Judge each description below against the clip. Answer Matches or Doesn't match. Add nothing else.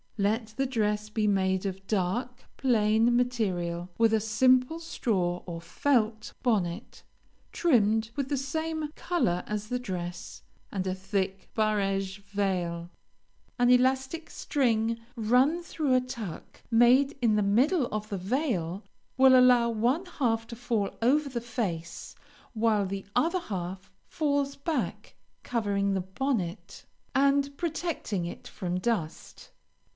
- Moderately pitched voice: Doesn't match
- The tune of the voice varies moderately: Matches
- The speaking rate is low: Matches